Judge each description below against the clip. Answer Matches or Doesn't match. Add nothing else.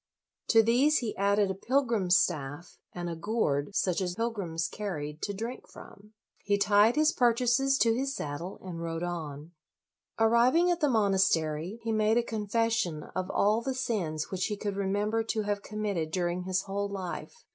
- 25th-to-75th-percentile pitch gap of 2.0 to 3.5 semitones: Doesn't match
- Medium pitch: Doesn't match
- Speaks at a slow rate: Doesn't match